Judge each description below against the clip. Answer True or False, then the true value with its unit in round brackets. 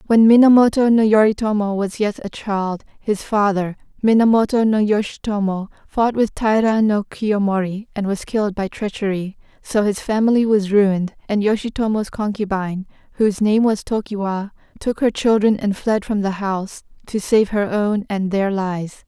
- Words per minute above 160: False (155 wpm)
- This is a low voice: False (210 Hz)